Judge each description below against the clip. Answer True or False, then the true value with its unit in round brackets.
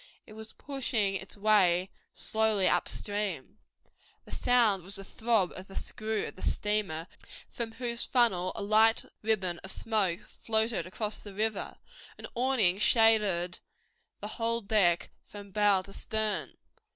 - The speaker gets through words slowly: False (145 wpm)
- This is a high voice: True (210 Hz)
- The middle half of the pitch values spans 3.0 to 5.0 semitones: False (2.6 semitones)